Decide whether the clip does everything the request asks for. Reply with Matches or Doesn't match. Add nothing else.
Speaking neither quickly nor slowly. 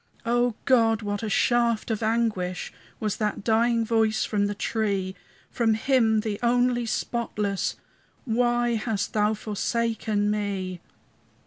Doesn't match